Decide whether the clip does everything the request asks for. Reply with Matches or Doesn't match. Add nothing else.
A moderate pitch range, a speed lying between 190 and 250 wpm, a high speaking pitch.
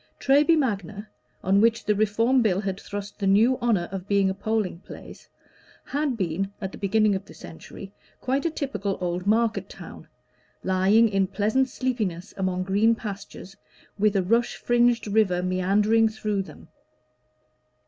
Doesn't match